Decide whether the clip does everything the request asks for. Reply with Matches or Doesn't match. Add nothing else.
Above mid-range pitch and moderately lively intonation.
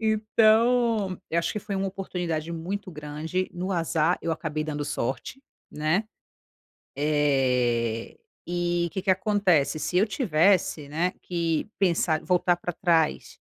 Doesn't match